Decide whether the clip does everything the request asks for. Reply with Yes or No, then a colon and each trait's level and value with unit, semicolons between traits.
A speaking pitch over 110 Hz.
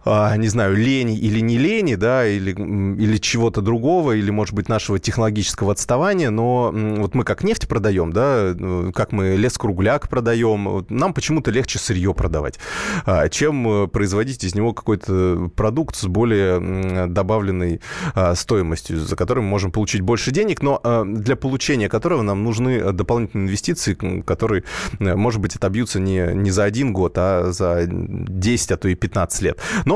No: low, 105 Hz